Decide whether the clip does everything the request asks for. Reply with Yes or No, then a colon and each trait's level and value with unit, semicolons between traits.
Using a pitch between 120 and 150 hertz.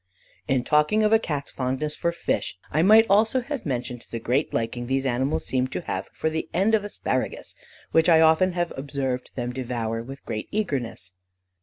Yes: medium, 140 Hz